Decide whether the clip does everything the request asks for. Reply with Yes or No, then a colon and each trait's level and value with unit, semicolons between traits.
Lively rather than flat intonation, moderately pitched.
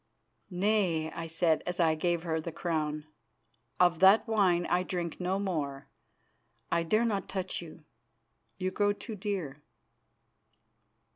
No: average, 3.2 semitones; medium, 175 Hz